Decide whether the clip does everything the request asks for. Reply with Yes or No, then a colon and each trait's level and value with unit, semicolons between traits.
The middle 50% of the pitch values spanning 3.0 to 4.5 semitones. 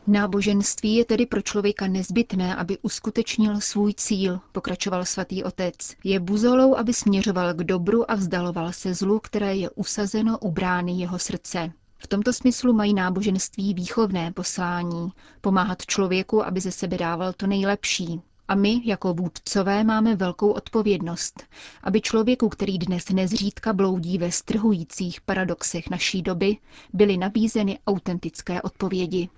No: narrow, 2.6 semitones